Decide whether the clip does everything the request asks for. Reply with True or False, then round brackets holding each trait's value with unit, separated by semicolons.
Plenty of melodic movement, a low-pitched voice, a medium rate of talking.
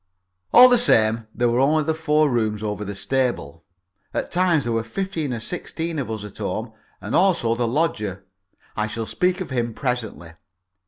True (6.5 semitones; 120 Hz; 180 wpm)